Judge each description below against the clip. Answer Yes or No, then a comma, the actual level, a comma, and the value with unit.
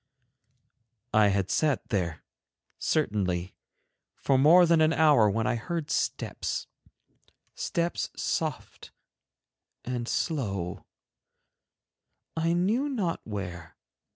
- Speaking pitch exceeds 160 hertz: No, low, 125 Hz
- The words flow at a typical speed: No, slow, 95 wpm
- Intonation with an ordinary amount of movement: No, wide, 8.8 semitones